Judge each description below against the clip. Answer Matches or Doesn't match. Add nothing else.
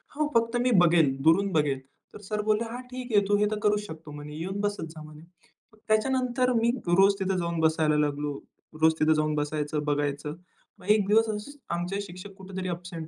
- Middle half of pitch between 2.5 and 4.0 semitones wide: Doesn't match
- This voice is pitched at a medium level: Matches